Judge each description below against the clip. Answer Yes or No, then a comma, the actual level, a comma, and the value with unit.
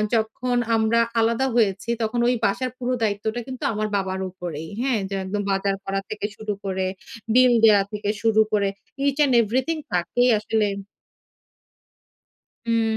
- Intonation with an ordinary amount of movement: Yes, average, 3.4 semitones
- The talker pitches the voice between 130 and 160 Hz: No, high, 220 Hz